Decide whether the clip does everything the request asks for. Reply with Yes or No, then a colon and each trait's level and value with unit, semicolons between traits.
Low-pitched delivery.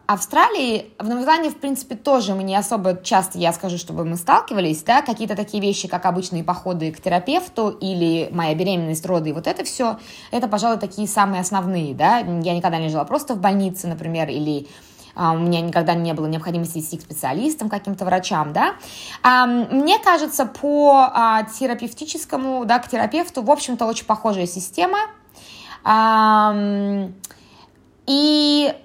No: high, 205 Hz